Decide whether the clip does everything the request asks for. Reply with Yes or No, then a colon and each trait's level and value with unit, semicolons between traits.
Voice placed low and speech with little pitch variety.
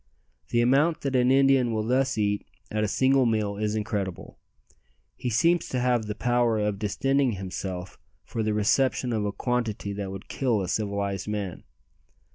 No: low, 110 Hz; average, 3.7 semitones